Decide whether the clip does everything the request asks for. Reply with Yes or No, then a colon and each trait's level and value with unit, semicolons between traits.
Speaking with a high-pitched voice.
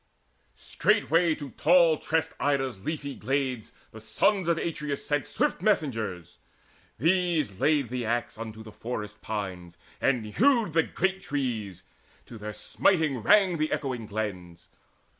No: low, 135 Hz